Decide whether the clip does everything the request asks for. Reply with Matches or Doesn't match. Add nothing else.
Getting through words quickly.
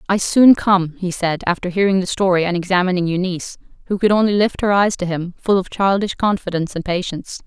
Matches